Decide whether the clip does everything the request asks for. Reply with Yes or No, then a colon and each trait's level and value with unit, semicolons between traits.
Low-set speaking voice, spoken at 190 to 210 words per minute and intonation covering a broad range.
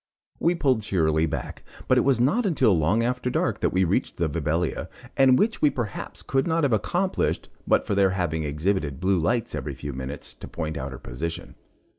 Yes: very low, 95 Hz; average, 200 wpm; wide, 8.5 semitones